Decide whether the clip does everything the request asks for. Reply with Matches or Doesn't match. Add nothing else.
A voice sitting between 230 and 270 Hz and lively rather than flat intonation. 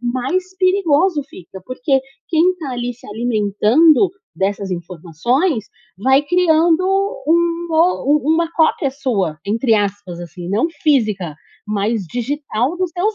Matches